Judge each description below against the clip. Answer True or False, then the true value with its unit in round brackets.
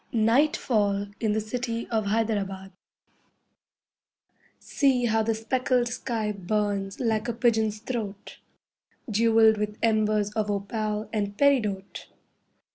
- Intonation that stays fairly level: True (1.9 semitones)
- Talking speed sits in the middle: False (110 wpm)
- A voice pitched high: True (220 Hz)